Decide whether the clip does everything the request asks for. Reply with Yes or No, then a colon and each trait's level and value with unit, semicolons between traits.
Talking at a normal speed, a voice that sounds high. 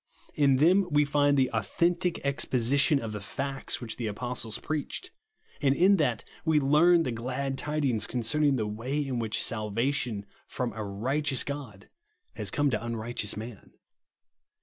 No: average, 150 wpm; low, 135 Hz